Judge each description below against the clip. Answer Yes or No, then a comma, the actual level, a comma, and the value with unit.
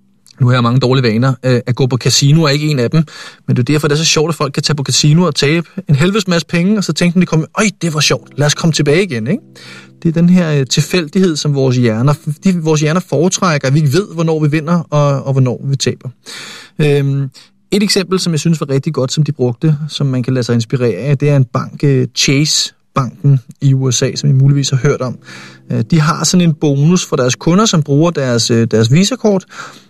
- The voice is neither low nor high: Yes, medium, 145 Hz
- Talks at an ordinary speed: No, fast, 235 wpm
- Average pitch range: Yes, average, 4.1 semitones